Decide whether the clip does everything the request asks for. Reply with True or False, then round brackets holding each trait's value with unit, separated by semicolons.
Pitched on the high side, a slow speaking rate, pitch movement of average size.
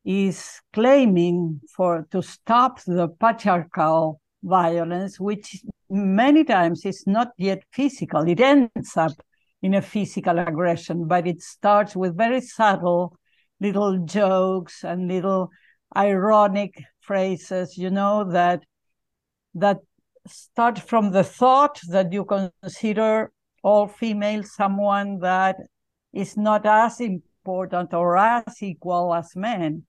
True (195 Hz; 115 wpm; 3.1 semitones)